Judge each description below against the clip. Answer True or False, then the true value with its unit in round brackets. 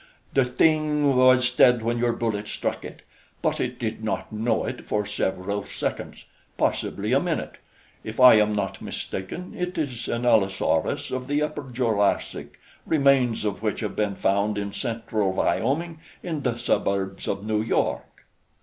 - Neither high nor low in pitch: False (115 Hz)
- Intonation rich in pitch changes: False (4.0 semitones)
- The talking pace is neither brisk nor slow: True (160 wpm)